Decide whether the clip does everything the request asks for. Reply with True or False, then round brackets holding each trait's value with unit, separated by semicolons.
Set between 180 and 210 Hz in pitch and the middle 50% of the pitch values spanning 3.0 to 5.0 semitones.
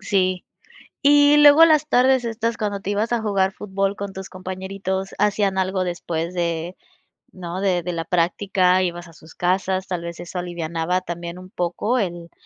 False (185 Hz; 2.6 semitones)